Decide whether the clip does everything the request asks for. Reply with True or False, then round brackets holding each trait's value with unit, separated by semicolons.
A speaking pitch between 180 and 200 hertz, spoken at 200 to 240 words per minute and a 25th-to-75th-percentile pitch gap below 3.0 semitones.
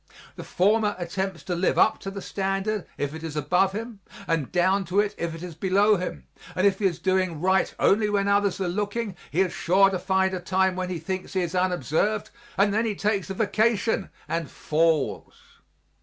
True (190 Hz; 205 wpm; 2.4 semitones)